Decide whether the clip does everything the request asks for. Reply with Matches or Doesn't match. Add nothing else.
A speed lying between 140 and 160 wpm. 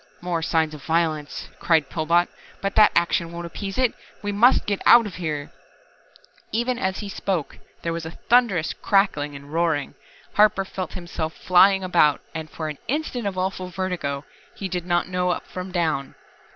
Doesn't match